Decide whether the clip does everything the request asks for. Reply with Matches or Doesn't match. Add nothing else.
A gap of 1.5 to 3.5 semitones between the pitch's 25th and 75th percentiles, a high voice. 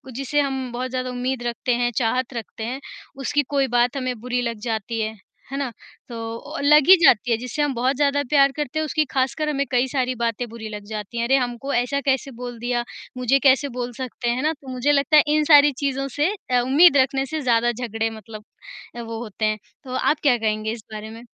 Matches